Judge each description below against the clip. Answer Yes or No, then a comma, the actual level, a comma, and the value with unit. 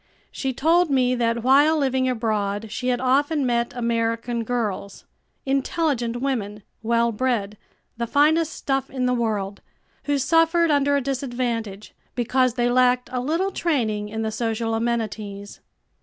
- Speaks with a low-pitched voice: No, high, 245 Hz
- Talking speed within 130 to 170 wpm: Yes, average, 140 wpm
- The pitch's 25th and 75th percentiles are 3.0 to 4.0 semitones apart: Yes, average, 3.3 semitones